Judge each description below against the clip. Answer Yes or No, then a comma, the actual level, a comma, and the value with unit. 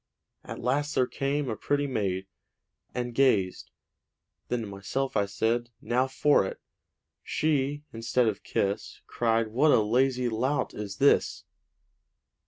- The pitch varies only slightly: No, average, 4.0 semitones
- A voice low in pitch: Yes, low, 120 Hz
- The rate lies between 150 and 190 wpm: No, slow, 135 wpm